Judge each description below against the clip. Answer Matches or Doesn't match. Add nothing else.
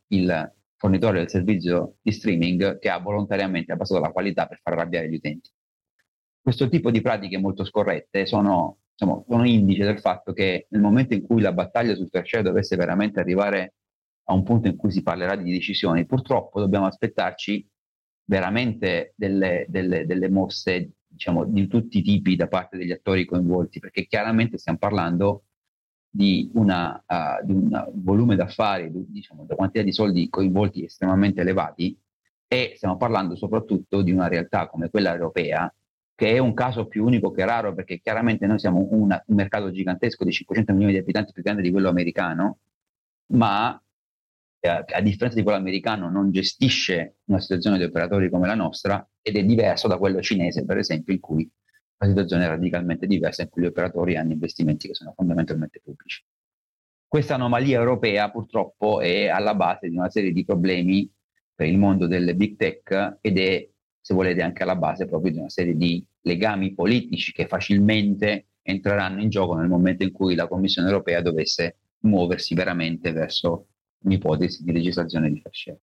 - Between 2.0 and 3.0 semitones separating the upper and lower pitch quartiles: Matches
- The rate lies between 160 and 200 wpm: Matches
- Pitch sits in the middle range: Doesn't match